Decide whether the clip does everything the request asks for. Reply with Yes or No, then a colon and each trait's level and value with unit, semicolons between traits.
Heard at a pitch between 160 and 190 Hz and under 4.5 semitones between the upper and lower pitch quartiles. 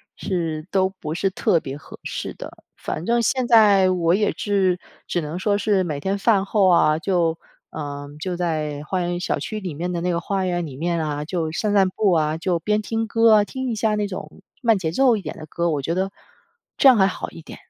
Yes: medium, 185 Hz; average, 4.0 semitones